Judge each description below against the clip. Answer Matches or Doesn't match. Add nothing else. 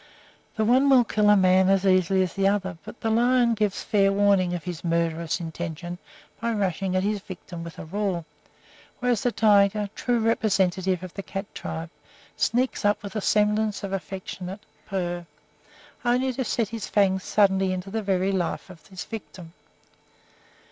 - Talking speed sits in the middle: Matches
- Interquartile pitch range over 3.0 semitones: Doesn't match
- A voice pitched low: Doesn't match